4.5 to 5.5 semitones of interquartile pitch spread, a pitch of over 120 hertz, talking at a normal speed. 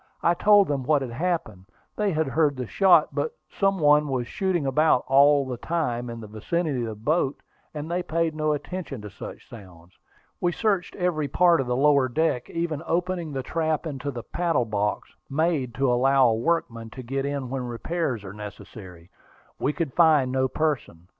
Yes: average, 5.2 semitones; medium, 140 Hz; average, 190 wpm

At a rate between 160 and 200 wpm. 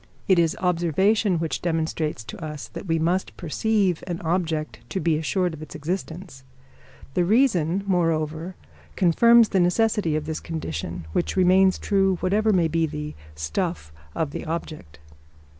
No: average, 150 wpm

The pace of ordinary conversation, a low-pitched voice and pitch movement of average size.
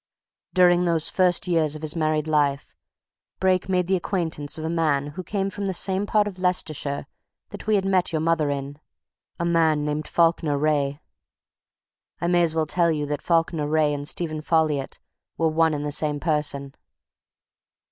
No: average, 180 wpm; medium, 160 Hz; average, 3.0 semitones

